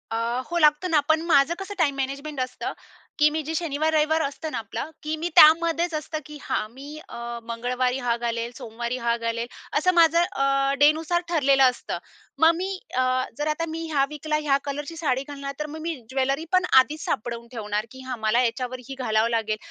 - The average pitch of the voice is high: Yes, very high, 280 Hz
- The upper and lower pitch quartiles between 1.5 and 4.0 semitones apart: No, average, 4.4 semitones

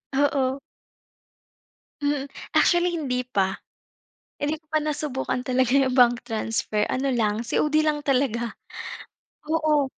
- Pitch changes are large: No, average, 3.1 semitones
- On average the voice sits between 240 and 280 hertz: Yes, very high, 265 Hz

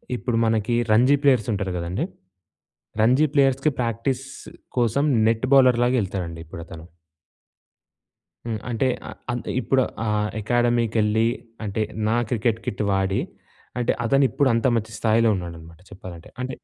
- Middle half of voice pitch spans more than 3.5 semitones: Yes, average, 4.2 semitones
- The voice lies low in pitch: Yes, low, 115 Hz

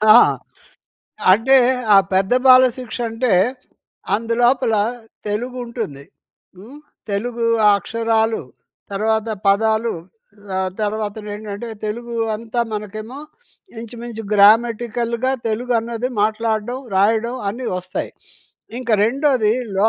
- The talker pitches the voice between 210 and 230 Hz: Yes, high, 225 Hz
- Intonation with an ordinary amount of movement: No, narrow, 2.2 semitones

